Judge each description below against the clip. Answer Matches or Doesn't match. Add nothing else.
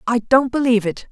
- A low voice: Doesn't match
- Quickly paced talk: Matches